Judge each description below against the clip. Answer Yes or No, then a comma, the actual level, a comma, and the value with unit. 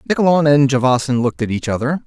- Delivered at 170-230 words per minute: Yes, fast, 205 wpm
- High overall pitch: No, low, 135 Hz